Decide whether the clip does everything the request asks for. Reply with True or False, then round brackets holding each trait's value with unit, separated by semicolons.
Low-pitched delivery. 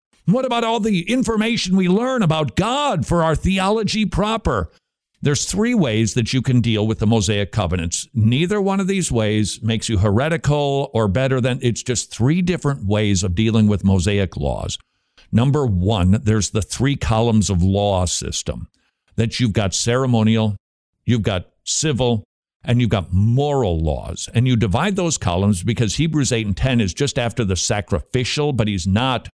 True (115 Hz)